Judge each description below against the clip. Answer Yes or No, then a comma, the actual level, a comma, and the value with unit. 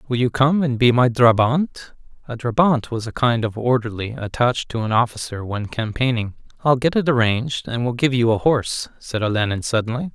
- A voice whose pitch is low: Yes, low, 120 Hz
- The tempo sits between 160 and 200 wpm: Yes, average, 195 wpm